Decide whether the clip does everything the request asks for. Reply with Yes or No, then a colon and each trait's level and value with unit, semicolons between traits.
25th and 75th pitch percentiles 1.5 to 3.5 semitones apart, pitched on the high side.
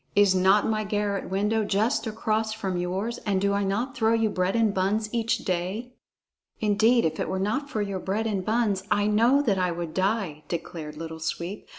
Yes: average, 2.9 semitones; high, 205 Hz